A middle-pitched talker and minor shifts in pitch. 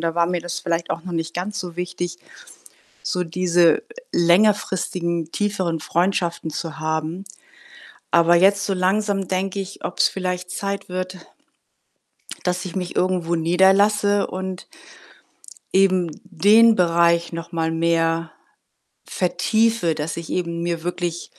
Yes: medium, 180 Hz; narrow, 2.1 semitones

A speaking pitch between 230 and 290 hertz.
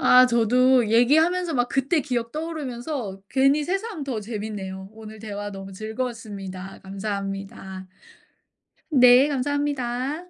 Yes: high, 240 Hz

